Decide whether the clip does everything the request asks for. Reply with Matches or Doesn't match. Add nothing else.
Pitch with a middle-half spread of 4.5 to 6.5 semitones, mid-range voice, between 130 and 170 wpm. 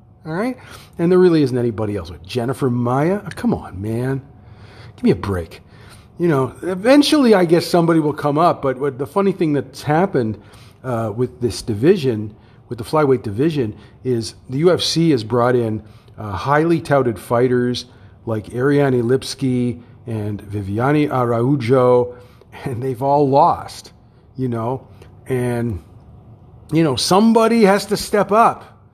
Doesn't match